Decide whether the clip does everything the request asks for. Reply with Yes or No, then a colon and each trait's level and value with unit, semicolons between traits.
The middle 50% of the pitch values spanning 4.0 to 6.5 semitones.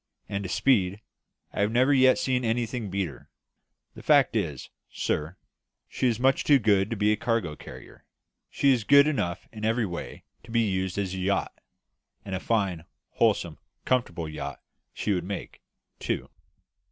Yes: average, 4.5 semitones